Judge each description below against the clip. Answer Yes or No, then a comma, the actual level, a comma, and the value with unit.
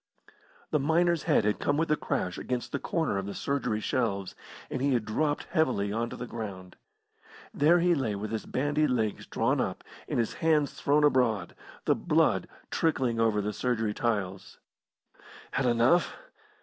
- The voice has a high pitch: No, low, 125 Hz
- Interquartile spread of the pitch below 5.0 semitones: No, wide, 5.5 semitones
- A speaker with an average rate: Yes, average, 170 wpm